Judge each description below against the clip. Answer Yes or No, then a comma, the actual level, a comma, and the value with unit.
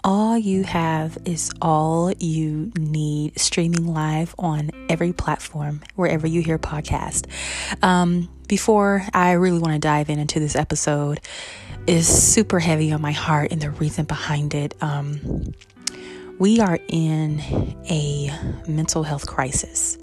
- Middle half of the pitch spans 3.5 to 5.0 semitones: No, narrow, 2.5 semitones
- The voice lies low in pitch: No, medium, 155 Hz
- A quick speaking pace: No, average, 140 wpm